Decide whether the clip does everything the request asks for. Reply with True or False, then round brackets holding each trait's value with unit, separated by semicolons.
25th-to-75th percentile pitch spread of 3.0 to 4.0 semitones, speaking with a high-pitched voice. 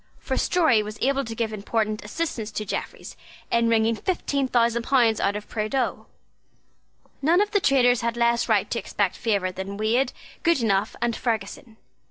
True (3.5 semitones; 230 Hz)